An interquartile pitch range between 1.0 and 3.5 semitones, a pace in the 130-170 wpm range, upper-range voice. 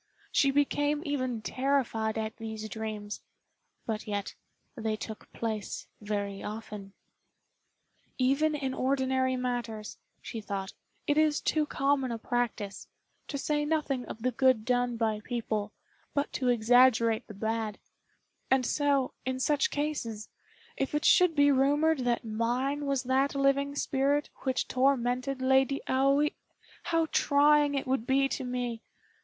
No: average, 3.9 semitones; slow, 135 wpm; very high, 255 Hz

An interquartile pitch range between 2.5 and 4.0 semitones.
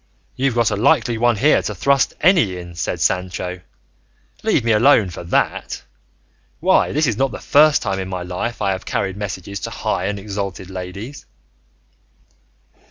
No: average, 4.6 semitones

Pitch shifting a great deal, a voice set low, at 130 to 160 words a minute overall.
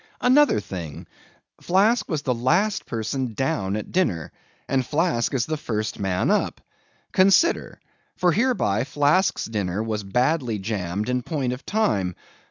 Yes: wide, 8.4 semitones; low, 125 Hz; average, 145 wpm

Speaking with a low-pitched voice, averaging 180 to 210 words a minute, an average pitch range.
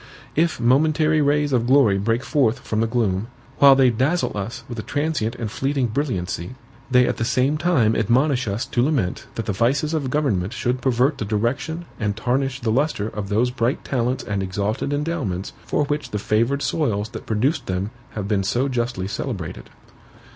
Yes: low, 120 Hz; average, 185 wpm; average, 4.7 semitones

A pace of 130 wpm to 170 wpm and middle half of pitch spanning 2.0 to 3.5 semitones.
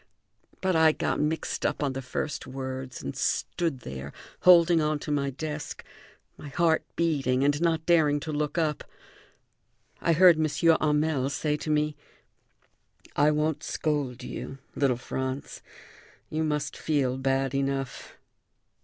Yes: average, 140 wpm; average, 2.7 semitones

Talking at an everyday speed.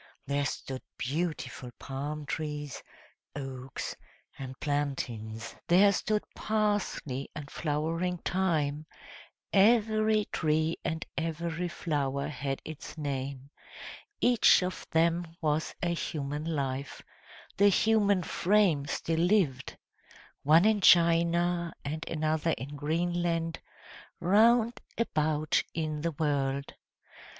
No: slow, 100 wpm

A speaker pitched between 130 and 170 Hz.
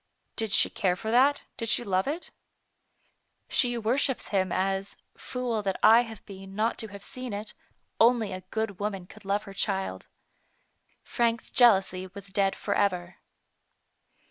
No: high, 205 Hz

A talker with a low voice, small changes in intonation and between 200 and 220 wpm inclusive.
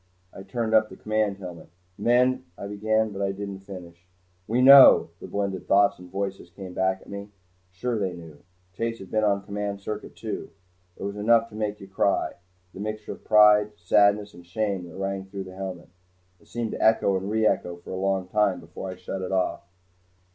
Yes: low, 100 Hz; narrow, 2.2 semitones; fast, 205 wpm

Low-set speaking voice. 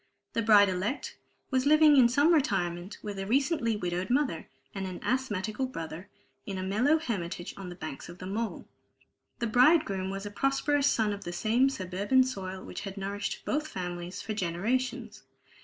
No: high, 205 Hz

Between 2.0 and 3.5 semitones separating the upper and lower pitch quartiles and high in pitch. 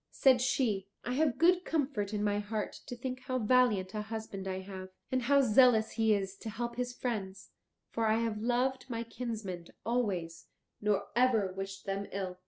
No: average, 4.1 semitones; high, 220 Hz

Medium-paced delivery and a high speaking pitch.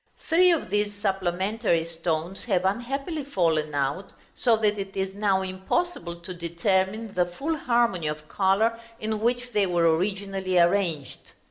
Yes: average, 145 wpm; high, 195 Hz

